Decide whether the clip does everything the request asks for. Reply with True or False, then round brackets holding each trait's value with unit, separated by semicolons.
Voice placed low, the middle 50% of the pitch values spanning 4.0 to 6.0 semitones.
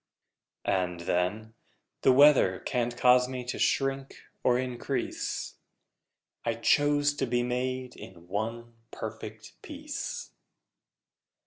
False (125 Hz; 3.1 semitones)